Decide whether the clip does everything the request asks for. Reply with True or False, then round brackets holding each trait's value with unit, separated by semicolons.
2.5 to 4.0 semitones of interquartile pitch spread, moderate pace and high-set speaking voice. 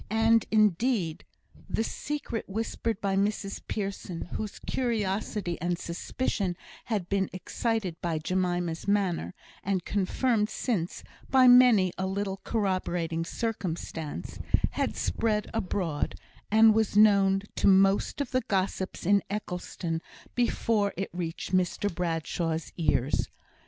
False (3.7 semitones; 115 wpm; 195 Hz)